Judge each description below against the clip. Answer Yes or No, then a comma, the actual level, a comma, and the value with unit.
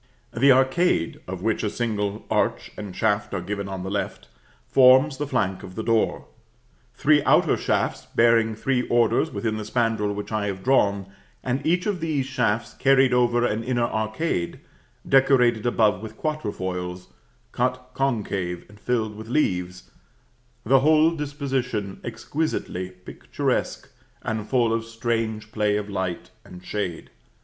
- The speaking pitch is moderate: No, low, 115 Hz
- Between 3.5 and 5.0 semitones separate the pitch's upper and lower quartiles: Yes, average, 4.2 semitones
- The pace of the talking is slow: No, average, 150 wpm